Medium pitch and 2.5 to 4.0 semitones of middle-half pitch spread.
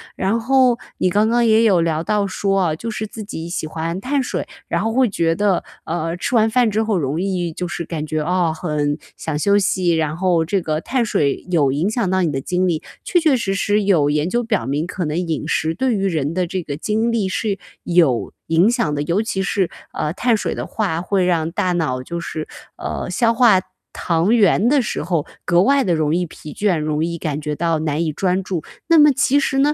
No: medium, 180 Hz; average, 5.2 semitones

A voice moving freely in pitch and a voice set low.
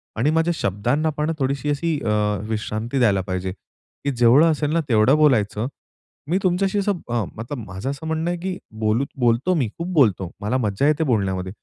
Yes: wide, 6.8 semitones; low, 130 Hz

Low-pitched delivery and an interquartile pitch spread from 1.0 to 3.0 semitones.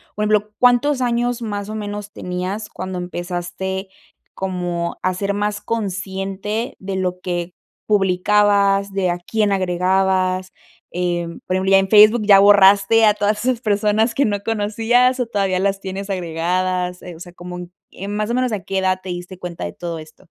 No: high, 195 Hz; narrow, 2.5 semitones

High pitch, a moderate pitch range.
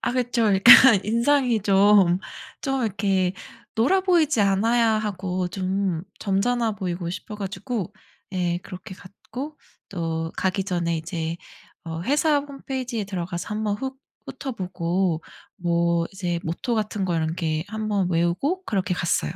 Yes: high, 195 Hz; average, 4.9 semitones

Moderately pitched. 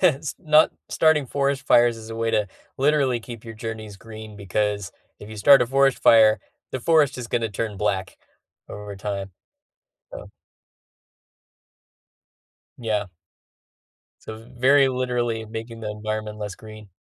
No: low, 115 Hz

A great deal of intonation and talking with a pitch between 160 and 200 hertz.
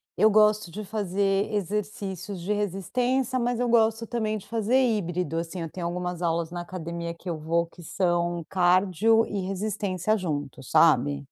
No: average, 3.9 semitones; high, 190 Hz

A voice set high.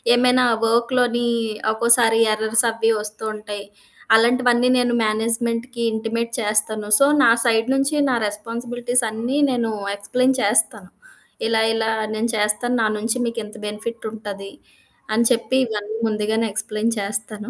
Yes: high, 225 Hz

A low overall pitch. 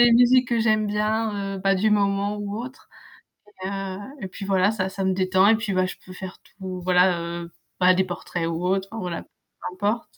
No: high, 195 Hz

